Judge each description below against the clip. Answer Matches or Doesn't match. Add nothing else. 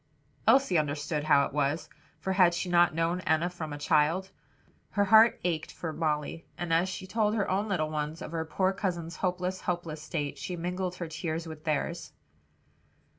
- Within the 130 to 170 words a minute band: Doesn't match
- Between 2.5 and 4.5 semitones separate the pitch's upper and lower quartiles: Matches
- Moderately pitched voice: Matches